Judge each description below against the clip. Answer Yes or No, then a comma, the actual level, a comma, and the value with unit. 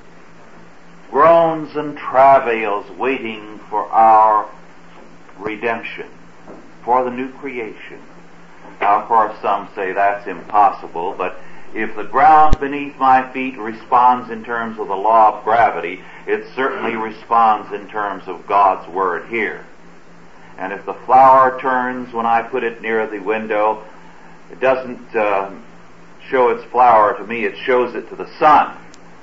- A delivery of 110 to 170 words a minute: Yes, average, 140 wpm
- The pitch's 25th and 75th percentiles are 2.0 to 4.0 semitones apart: Yes, average, 3.0 semitones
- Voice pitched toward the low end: Yes, low, 120 Hz